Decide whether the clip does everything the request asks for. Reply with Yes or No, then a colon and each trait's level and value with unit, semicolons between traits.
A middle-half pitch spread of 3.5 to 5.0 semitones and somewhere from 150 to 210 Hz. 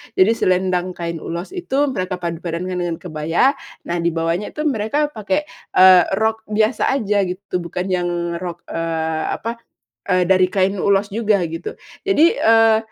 Yes: average, 4.1 semitones; medium, 185 Hz